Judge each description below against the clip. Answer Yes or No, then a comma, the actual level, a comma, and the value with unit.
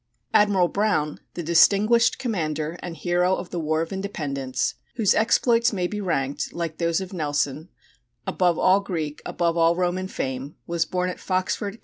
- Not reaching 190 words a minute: Yes, average, 165 wpm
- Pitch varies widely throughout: No, average, 3.7 semitones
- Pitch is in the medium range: Yes, medium, 175 Hz